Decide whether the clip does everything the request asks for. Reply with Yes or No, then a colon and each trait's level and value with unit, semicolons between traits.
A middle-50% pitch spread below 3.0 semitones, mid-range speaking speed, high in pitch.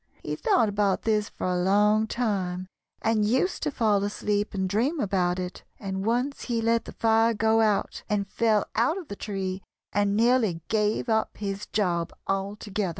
Yes: narrow, 2.5 semitones; average, 175 wpm; high, 210 Hz